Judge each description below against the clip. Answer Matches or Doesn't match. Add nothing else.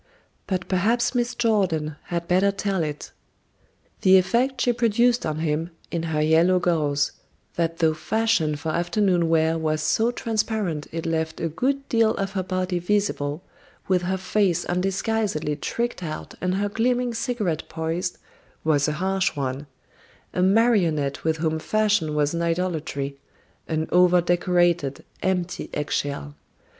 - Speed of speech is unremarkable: Matches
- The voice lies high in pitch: Doesn't match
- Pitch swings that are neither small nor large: Matches